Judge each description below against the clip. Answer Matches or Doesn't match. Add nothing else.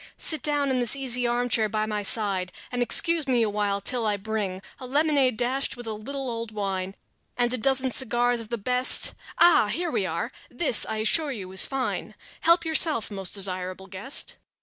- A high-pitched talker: Matches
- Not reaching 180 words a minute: Doesn't match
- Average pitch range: Matches